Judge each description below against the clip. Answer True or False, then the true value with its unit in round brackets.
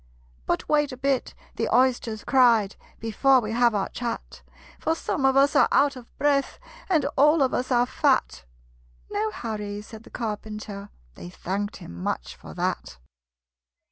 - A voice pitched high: True (240 Hz)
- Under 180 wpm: True (160 wpm)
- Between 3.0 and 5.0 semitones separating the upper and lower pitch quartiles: True (4.3 semitones)